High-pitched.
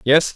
No: medium, 145 Hz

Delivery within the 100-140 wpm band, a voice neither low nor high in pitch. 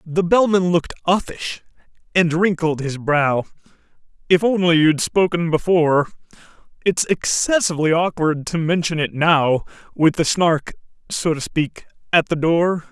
Yes: slow, 135 wpm; medium, 165 Hz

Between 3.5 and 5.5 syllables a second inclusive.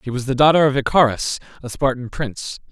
No: 6.2 syllables/s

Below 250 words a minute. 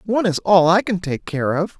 No: fast, 265 wpm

